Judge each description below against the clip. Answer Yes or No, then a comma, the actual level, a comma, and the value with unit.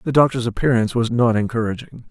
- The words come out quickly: No, average, 170 wpm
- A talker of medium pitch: No, low, 120 Hz